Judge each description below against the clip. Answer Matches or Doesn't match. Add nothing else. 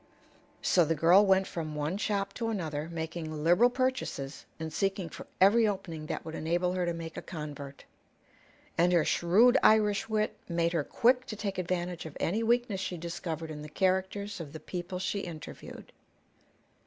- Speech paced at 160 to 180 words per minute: Matches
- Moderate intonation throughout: Matches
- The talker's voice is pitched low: Doesn't match